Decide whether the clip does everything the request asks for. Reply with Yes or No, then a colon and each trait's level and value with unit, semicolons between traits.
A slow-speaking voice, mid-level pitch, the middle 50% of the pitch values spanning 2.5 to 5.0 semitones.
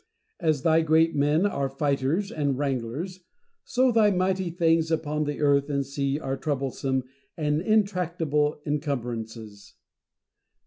Yes: slow, 125 wpm; medium, 150 Hz; average, 3.3 semitones